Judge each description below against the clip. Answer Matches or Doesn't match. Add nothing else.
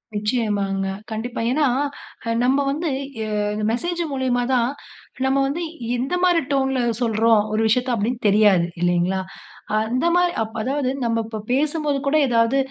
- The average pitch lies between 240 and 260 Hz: Matches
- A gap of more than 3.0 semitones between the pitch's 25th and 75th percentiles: Matches